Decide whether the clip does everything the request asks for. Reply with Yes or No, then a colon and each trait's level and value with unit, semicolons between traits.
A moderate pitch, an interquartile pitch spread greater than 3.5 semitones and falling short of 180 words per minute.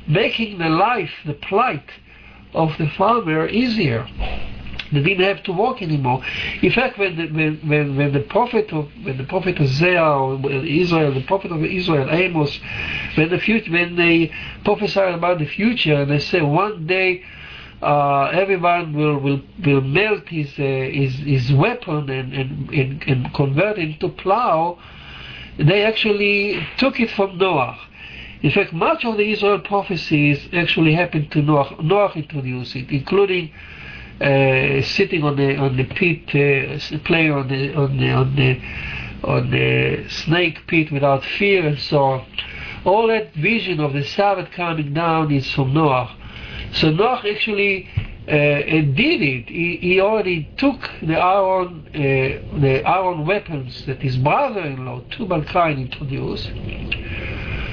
Yes: medium, 155 Hz; average, 5.2 semitones; average, 155 wpm